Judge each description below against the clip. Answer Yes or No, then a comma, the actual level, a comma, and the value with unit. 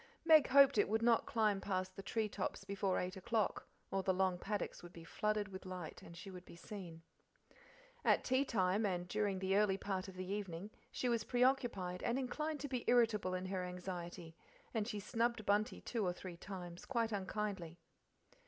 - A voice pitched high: Yes, high, 195 Hz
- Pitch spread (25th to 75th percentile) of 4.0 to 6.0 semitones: No, average, 3.5 semitones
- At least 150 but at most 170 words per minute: No, average, 190 wpm